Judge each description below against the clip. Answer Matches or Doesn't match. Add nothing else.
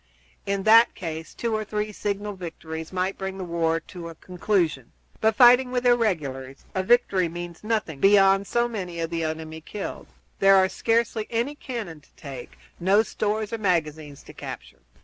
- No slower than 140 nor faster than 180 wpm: Matches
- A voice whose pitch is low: Doesn't match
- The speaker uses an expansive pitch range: Doesn't match